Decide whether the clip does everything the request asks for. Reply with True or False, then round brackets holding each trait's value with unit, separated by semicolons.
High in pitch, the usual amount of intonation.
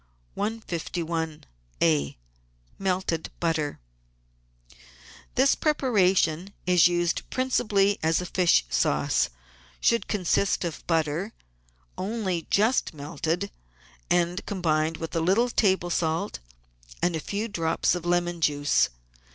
False (175 Hz; 3.6 semitones)